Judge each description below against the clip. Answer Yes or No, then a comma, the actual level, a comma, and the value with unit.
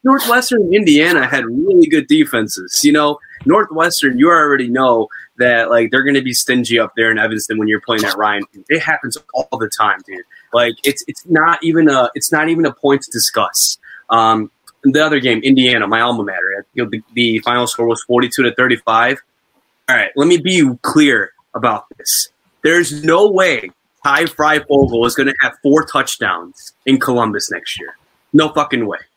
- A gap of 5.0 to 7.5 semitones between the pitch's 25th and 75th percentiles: Yes, wide, 5.5 semitones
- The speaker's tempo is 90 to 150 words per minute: No, average, 190 wpm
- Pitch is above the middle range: No, low, 135 Hz